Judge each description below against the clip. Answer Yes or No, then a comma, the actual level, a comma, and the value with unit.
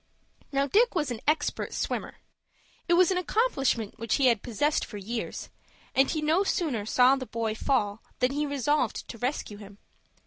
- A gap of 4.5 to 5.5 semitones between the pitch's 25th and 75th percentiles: Yes, average, 4.9 semitones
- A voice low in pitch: No, very high, 270 Hz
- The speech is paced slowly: No, average, 175 wpm